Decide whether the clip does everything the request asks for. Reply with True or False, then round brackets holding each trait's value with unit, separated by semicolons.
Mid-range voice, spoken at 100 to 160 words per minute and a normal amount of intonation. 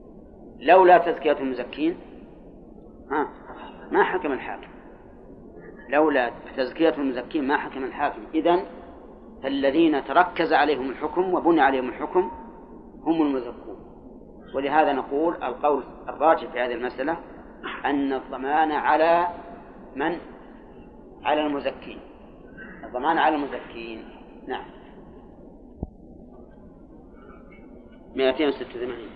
False (145 Hz; 90 wpm; 3.8 semitones)